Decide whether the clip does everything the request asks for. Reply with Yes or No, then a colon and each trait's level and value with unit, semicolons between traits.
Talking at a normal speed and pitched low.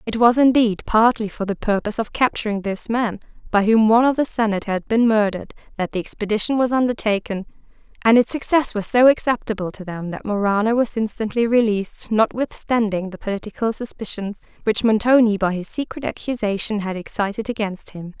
No: average, 170 wpm; high, 220 Hz